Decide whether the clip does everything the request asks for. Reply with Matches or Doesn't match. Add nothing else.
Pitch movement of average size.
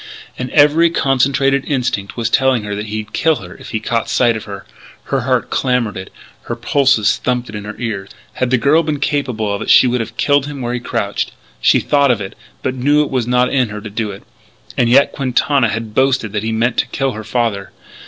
Matches